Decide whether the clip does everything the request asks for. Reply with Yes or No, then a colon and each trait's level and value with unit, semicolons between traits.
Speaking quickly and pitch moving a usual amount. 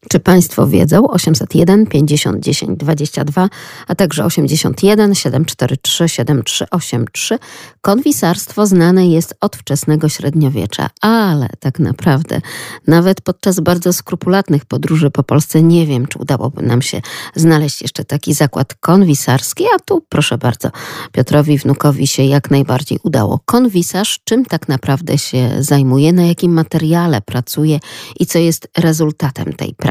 No: average, 130 wpm; average, 4.0 semitones